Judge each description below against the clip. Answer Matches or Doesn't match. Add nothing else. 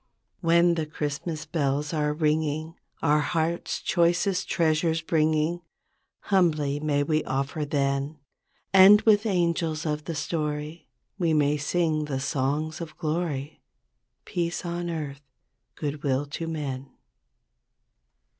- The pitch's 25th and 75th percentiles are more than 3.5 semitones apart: Doesn't match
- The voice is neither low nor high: Matches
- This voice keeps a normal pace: Doesn't match